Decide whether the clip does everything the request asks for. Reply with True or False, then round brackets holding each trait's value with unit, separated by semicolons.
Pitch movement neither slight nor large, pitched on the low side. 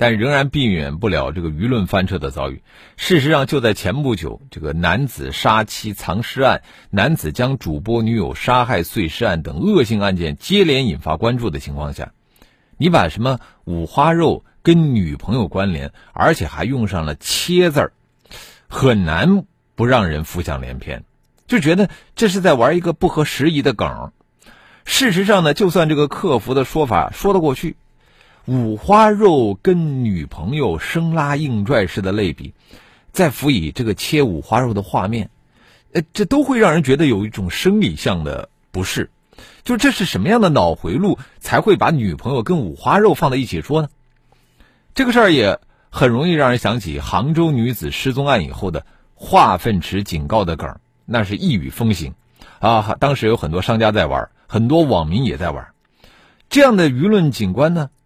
False (8.5 semitones; 125 Hz)